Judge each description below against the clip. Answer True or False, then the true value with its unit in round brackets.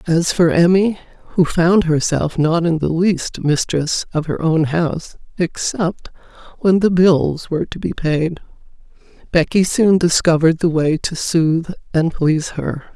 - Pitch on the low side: False (165 Hz)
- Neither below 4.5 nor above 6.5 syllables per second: False (4.1 syllables/s)